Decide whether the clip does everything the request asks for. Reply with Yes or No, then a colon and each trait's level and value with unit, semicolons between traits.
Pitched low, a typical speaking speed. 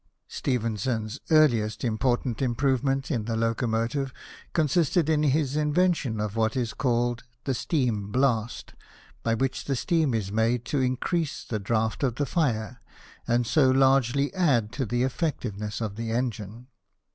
Yes: low, 125 Hz; average, 145 wpm